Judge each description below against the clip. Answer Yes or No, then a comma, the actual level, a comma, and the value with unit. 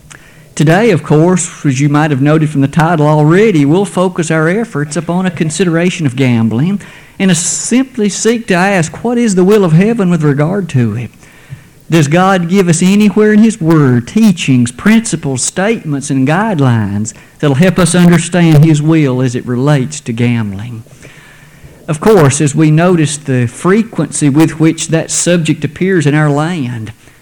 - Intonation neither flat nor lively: Yes, average, 4.2 semitones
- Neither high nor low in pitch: Yes, medium, 160 Hz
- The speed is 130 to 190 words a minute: Yes, average, 170 wpm